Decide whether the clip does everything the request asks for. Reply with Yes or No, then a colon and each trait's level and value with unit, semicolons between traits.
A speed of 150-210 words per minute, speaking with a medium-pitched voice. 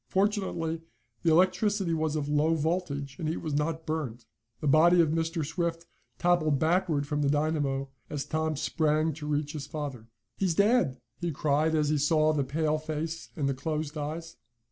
Yes: average, 175 wpm; medium, 155 Hz